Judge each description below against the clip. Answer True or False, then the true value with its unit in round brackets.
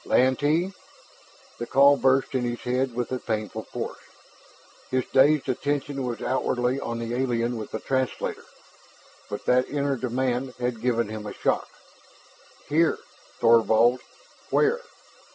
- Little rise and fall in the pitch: True (2.3 semitones)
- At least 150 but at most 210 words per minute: False (135 wpm)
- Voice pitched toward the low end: True (125 Hz)